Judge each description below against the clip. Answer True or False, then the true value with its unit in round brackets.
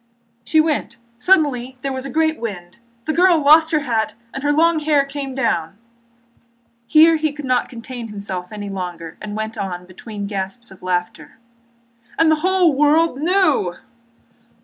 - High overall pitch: True (265 Hz)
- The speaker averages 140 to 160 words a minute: True (155 wpm)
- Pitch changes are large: True (7.4 semitones)